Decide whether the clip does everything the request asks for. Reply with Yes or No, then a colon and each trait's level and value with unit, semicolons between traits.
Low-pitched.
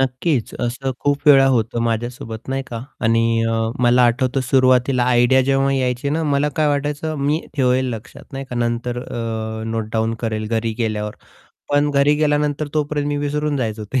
Yes: low, 130 Hz